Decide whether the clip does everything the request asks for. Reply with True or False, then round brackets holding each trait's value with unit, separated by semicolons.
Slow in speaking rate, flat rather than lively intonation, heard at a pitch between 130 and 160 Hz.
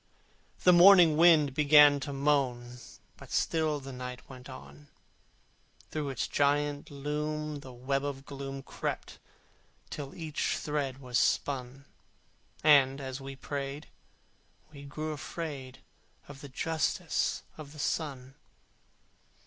True (120 wpm; 2.1 semitones; 140 Hz)